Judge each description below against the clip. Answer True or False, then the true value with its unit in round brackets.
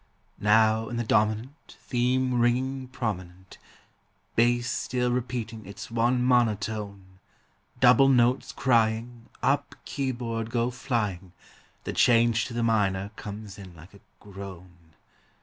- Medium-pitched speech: False (115 Hz)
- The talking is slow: True (115 wpm)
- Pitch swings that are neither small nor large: True (3.2 semitones)